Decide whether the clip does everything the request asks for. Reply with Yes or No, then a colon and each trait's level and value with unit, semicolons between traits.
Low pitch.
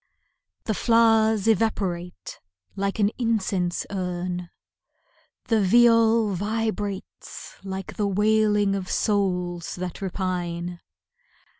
No: high, 200 Hz